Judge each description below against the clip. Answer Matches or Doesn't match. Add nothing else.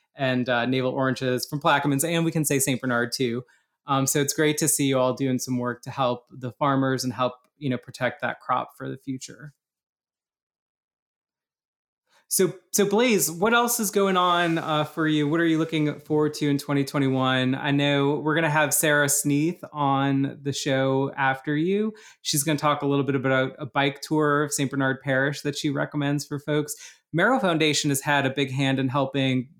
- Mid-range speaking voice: Matches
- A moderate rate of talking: Matches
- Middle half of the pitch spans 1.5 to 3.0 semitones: Matches